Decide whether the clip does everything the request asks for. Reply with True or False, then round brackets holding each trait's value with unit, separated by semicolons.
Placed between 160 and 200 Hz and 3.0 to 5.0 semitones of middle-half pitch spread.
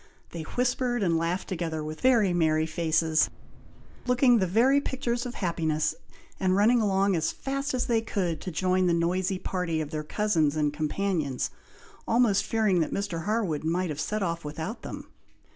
False (185 Hz; 5.5 semitones)